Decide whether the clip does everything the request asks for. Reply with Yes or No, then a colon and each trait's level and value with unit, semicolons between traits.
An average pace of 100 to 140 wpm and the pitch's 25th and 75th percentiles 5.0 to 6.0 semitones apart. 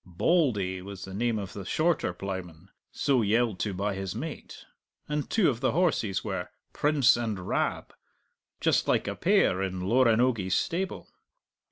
No: average, 155 wpm; wide, 5.6 semitones